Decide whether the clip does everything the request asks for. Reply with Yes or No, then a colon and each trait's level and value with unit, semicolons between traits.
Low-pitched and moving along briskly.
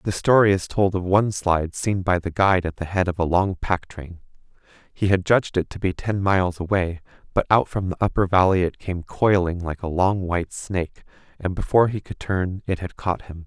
Yes: very low, 90 Hz; fast, 225 wpm